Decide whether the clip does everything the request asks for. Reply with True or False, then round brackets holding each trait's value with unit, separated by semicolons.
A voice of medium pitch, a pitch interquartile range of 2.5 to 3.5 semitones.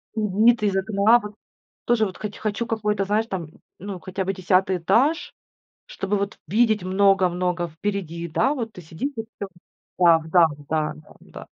False (195 Hz; 3.2 semitones)